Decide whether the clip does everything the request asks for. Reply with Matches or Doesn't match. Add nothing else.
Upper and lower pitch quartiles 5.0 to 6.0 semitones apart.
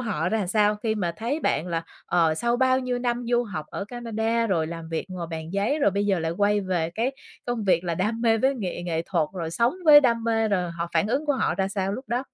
Matches